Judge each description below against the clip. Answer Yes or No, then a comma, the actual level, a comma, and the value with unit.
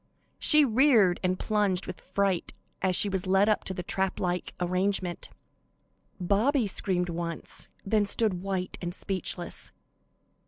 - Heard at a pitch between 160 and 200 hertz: Yes, high, 190 Hz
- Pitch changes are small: Yes, narrow, 2.3 semitones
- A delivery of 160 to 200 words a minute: No, slow, 135 wpm